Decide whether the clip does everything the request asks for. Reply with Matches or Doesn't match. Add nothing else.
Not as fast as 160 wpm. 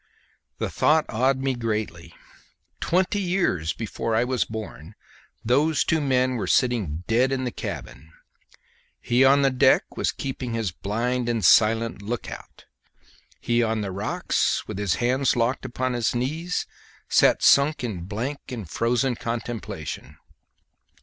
Matches